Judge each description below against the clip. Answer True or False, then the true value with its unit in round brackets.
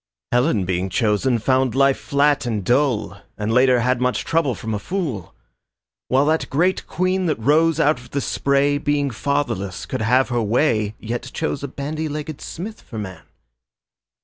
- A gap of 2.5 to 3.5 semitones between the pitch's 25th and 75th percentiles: False (4.7 semitones)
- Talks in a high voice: False (130 Hz)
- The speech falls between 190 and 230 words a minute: False (170 wpm)